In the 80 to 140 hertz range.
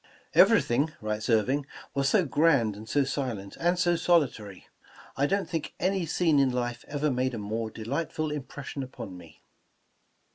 Yes: low, 135 Hz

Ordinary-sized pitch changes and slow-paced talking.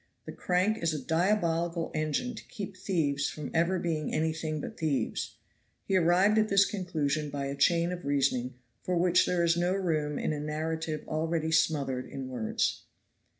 No: average, 3.2 semitones; average, 170 wpm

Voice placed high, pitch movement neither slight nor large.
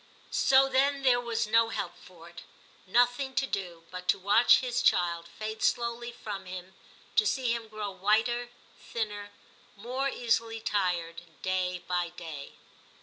Yes: high, 215 Hz; average, 4.8 semitones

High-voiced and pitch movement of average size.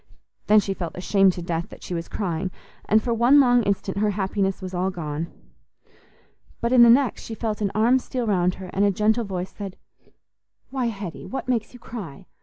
Yes: high, 200 Hz; average, 4.0 semitones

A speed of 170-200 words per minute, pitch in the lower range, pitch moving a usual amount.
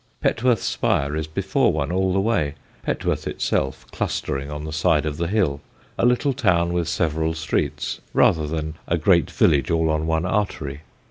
Yes: average, 175 wpm; very low, 80 Hz; average, 3.4 semitones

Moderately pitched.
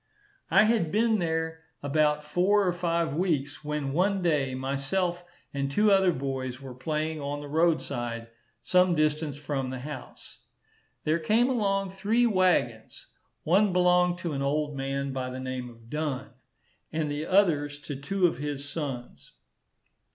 Yes: medium, 150 Hz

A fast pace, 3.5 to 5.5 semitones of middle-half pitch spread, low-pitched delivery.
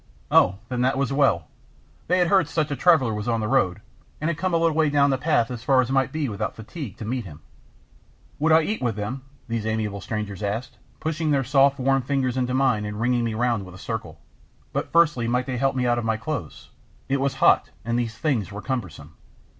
Yes: fast, 230 wpm; average, 4.1 semitones; low, 125 Hz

